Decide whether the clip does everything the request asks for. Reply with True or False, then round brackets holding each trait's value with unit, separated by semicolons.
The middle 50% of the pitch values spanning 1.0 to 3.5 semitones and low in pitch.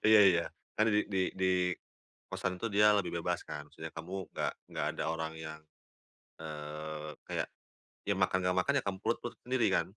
False (4.8 semitones; 90 Hz)